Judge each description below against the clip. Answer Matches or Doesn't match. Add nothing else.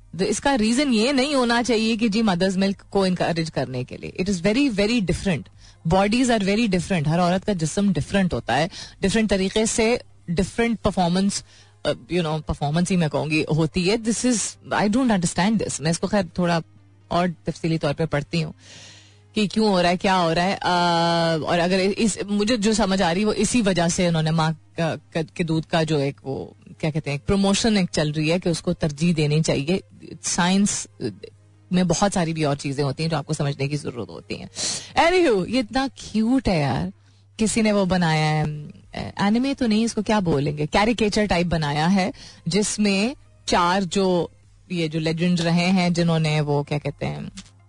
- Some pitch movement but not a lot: Matches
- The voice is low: Doesn't match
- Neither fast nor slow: Doesn't match